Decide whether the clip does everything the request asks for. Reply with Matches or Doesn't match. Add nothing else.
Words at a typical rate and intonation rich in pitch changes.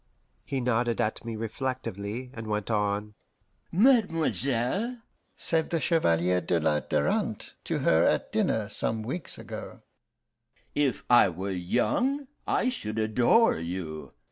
Doesn't match